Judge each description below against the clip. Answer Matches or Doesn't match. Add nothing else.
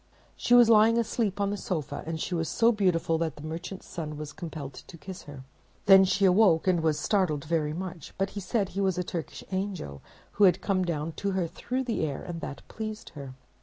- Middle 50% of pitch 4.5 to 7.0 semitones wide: Doesn't match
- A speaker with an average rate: Doesn't match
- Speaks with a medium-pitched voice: Matches